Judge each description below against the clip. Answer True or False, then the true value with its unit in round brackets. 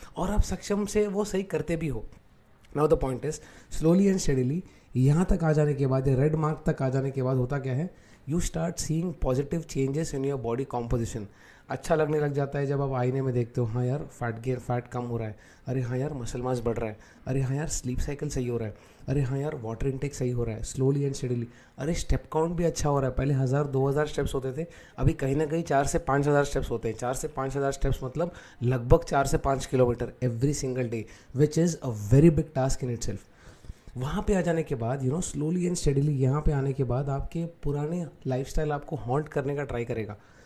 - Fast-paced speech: True (245 wpm)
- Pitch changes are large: False (3.6 semitones)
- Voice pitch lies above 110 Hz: True (135 Hz)